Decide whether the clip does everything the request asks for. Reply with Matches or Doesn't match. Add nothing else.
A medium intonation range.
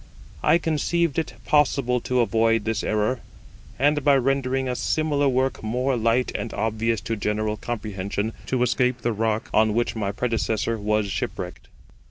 Matches